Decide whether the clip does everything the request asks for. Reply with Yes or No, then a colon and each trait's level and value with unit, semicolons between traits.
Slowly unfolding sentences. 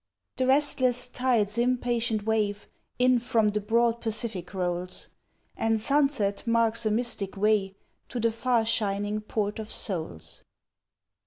Yes: slow, 130 wpm